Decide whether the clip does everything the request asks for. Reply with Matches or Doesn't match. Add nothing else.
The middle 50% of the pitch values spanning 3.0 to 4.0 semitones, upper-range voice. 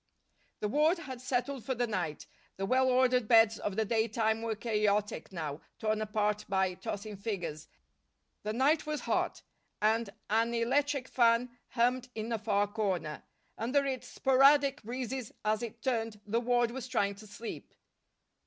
Matches